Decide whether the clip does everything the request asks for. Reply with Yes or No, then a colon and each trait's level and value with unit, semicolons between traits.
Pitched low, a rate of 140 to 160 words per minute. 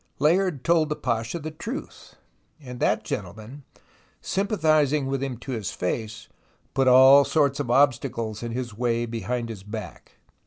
Yes: low, 130 Hz; average, 155 wpm